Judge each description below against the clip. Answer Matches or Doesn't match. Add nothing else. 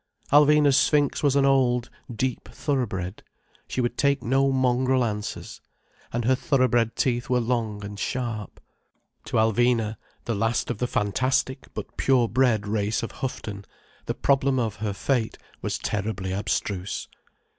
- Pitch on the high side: Doesn't match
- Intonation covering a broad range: Doesn't match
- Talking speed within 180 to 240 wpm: Doesn't match